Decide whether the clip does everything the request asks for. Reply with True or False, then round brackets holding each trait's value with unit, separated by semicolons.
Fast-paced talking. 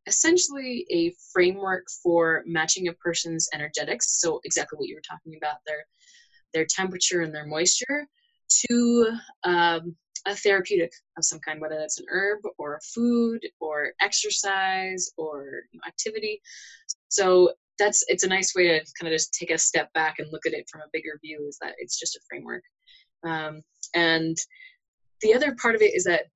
False (180 wpm)